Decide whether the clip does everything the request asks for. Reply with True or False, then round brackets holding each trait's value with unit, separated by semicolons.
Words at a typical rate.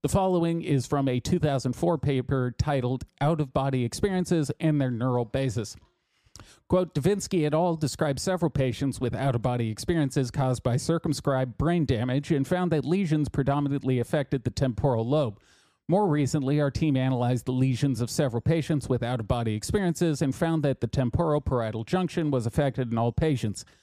True (175 wpm)